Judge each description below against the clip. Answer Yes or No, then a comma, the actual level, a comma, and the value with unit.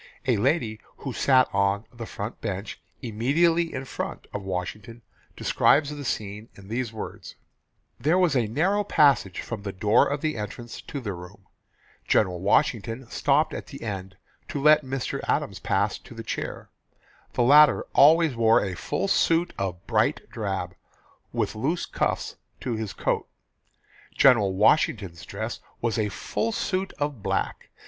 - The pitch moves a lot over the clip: Yes, wide, 6.3 semitones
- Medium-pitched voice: No, low, 115 Hz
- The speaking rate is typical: Yes, average, 155 wpm